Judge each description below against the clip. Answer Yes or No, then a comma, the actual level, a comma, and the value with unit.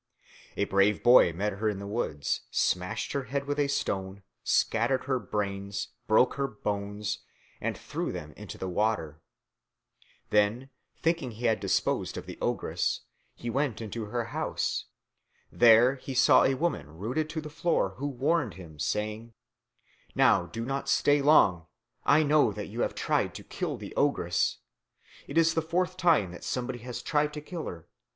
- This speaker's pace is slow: No, average, 170 wpm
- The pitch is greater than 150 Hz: No, low, 120 Hz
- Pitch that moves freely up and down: Yes, wide, 5.8 semitones